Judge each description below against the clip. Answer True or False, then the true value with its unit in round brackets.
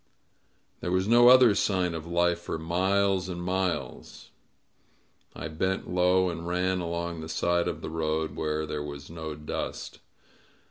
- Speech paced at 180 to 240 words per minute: False (150 wpm)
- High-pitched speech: False (85 Hz)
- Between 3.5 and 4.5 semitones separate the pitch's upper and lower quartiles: False (2.7 semitones)